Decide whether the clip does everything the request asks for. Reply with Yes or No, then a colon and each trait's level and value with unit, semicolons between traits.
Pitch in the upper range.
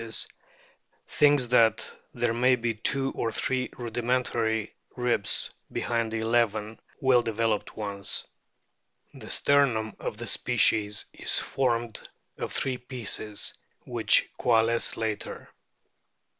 No: low, 115 Hz